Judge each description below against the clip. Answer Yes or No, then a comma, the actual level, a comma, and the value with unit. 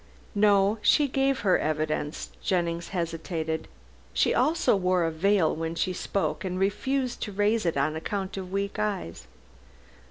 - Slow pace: No, average, 150 wpm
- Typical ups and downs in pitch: Yes, average, 4.0 semitones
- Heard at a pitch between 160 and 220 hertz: Yes, high, 190 Hz